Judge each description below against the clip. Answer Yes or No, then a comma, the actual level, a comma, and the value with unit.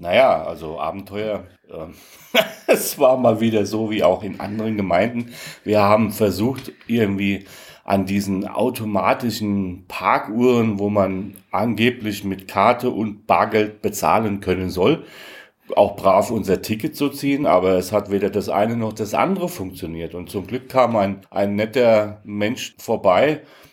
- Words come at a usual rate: Yes, average, 145 wpm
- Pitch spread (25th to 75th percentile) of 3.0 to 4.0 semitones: No, narrow, 2.6 semitones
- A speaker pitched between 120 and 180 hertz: No, low, 105 Hz